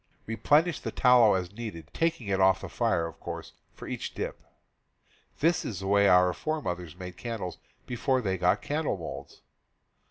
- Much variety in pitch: Yes, wide, 5.7 semitones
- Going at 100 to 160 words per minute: No, average, 170 wpm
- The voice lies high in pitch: No, low, 100 Hz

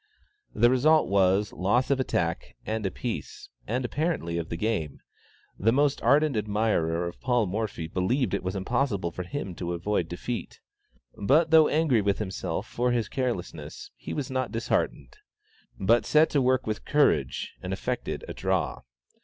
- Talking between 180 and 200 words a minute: No, average, 160 wpm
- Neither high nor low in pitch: No, low, 110 Hz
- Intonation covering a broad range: Yes, wide, 5.9 semitones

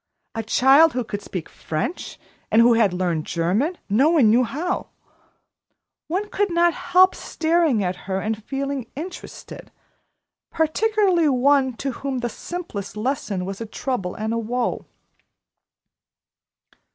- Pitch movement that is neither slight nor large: No, wide, 7.2 semitones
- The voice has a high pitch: Yes, very high, 250 Hz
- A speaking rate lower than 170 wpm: Yes, slow, 135 wpm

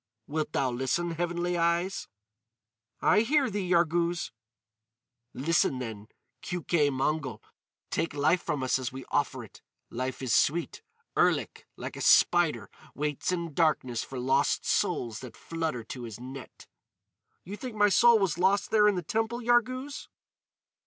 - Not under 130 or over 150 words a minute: Yes, average, 145 wpm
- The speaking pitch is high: No, medium, 165 Hz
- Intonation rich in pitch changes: Yes, wide, 6.1 semitones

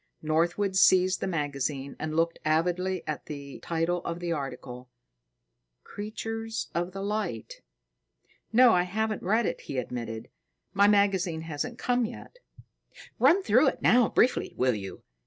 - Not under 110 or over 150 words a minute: Yes, average, 140 wpm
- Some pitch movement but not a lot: No, wide, 5.7 semitones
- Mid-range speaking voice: Yes, medium, 175 Hz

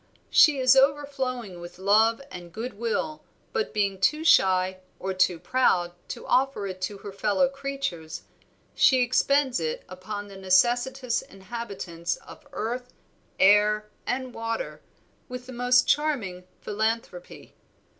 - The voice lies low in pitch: No, high, 225 Hz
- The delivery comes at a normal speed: No, slow, 130 wpm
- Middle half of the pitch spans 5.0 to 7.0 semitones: Yes, wide, 5.4 semitones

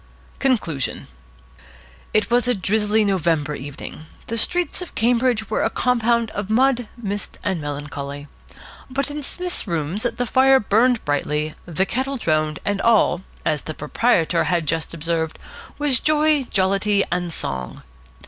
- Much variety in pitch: Yes, wide, 7.6 semitones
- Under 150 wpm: Yes, average, 140 wpm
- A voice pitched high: Yes, high, 205 Hz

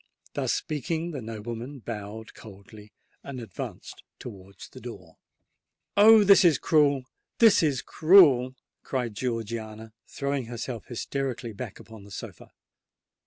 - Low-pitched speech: Yes, low, 120 Hz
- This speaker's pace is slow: Yes, slow, 120 wpm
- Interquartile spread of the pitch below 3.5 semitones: No, average, 4.4 semitones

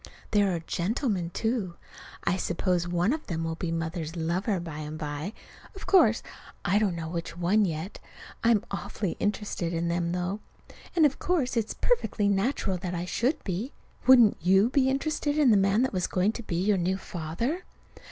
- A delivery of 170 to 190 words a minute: Yes, average, 185 wpm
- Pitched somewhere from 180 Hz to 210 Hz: Yes, high, 190 Hz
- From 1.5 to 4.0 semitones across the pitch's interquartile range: No, average, 5.2 semitones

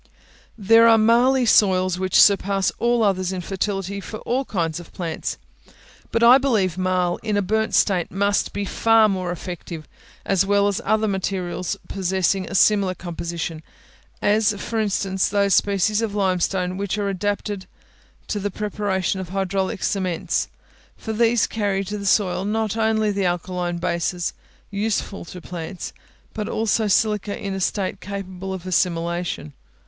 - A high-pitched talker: Yes, high, 195 Hz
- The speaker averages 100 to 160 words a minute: Yes, average, 155 wpm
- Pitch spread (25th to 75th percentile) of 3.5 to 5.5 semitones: No, narrow, 2.4 semitones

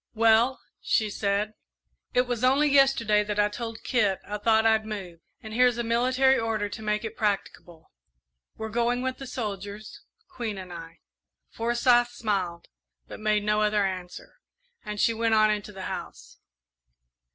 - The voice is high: Yes, high, 220 Hz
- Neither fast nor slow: Yes, average, 160 wpm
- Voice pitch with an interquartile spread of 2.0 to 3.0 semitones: Yes, narrow, 2.5 semitones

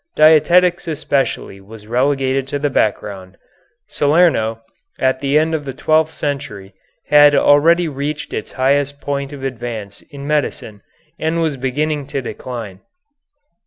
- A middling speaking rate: No, slow, 130 wpm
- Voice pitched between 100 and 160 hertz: Yes, medium, 140 Hz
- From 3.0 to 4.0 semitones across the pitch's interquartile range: Yes, average, 3.6 semitones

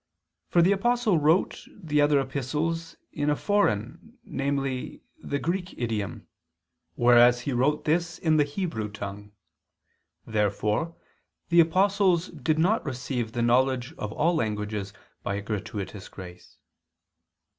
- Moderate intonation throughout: No, wide, 7.2 semitones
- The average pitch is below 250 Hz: Yes, medium, 140 Hz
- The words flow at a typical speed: No, slow, 125 wpm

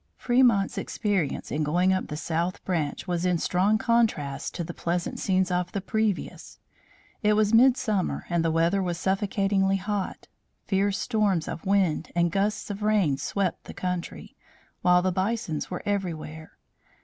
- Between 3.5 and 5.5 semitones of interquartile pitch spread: No, average, 3.0 semitones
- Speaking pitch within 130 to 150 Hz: No, medium, 185 Hz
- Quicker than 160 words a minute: No, average, 155 wpm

